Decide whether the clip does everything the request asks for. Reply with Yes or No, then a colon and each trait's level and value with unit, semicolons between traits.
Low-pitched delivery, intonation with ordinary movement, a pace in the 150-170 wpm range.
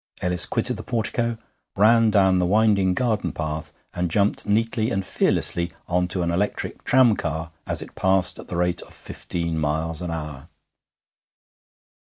Yes: very low, 90 Hz; average, 4.2 semitones; average, 155 wpm